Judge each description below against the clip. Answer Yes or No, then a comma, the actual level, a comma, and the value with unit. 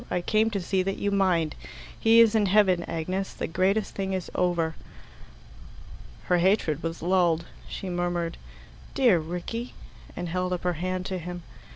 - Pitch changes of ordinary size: No, narrow, 2.3 semitones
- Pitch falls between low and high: Yes, medium, 180 Hz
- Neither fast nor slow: Yes, average, 165 wpm